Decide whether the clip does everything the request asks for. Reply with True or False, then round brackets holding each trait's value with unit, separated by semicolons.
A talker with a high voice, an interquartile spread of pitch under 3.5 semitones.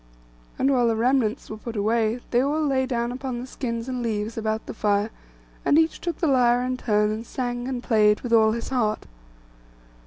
True (240 Hz; 2.8 semitones)